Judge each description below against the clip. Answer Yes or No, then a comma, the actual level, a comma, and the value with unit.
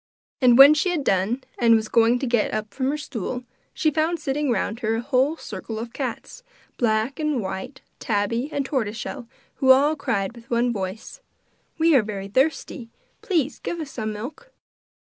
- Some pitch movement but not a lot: Yes, average, 4.7 semitones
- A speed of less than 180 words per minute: No, average, 185 wpm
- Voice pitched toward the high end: Yes, high, 245 Hz